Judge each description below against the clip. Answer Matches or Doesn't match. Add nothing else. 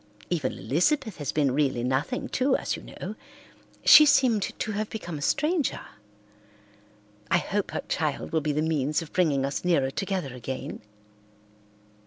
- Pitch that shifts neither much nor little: Doesn't match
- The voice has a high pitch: Doesn't match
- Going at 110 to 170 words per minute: Matches